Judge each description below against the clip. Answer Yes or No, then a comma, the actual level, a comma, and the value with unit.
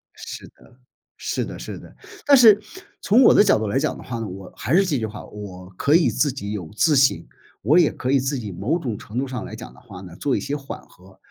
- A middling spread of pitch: No, wide, 6.2 semitones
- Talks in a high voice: No, low, 125 Hz